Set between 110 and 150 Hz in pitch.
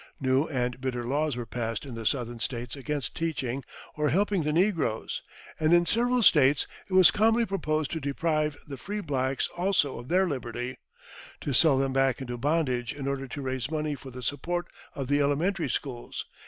Yes: medium, 140 Hz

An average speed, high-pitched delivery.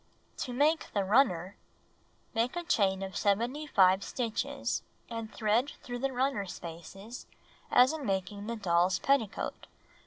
No: slow, 130 wpm; high, 225 Hz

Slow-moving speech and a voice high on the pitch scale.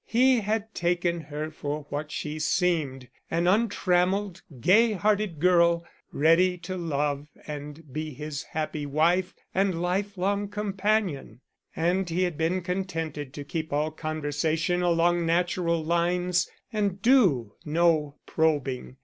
No: slow, 125 wpm; medium, 170 Hz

